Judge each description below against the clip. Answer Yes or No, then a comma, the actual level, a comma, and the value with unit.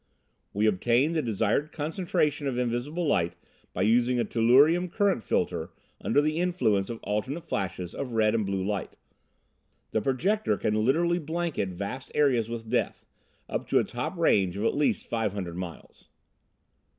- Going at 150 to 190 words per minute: Yes, average, 160 wpm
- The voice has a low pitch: Yes, low, 120 Hz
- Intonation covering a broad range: Yes, wide, 6.6 semitones